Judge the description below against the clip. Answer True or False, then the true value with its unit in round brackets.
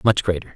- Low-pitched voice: True (95 Hz)